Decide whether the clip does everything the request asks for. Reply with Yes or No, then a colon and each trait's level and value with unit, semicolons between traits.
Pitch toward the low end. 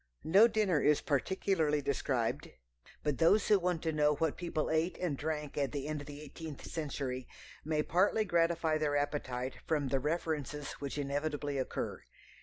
No: medium, 150 Hz